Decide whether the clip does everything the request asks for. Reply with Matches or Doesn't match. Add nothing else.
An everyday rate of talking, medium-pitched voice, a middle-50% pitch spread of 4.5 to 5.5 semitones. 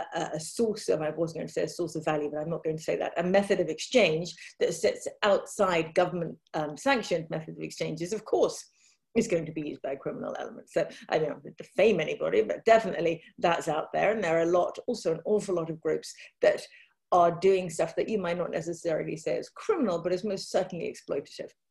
Doesn't match